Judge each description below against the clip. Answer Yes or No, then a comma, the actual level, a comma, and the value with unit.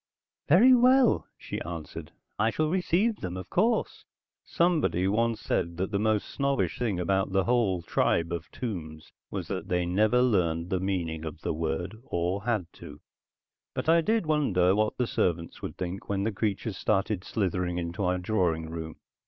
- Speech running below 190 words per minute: Yes, average, 170 wpm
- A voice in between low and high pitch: No, very low, 95 Hz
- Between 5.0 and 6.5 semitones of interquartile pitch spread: Yes, wide, 5.4 semitones